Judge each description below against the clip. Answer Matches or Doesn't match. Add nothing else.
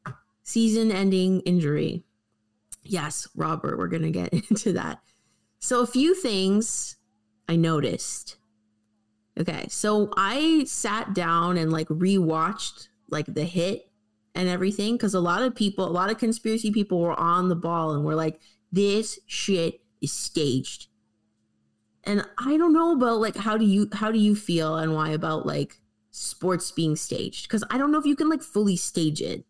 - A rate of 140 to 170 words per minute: Matches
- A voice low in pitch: Doesn't match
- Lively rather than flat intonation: Matches